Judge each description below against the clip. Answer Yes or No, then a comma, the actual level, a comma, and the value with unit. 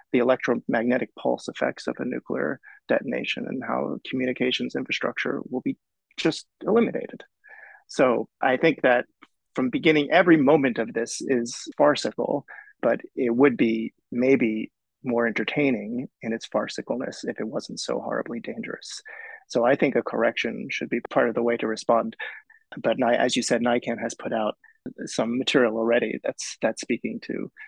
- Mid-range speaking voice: No, low, 125 Hz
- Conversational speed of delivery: Yes, average, 155 wpm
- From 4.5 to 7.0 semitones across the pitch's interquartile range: No, average, 4.0 semitones